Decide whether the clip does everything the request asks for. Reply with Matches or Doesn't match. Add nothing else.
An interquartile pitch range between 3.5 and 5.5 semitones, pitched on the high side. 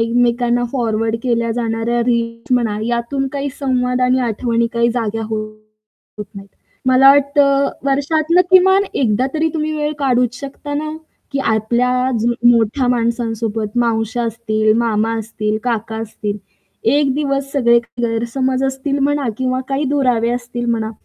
Doesn't match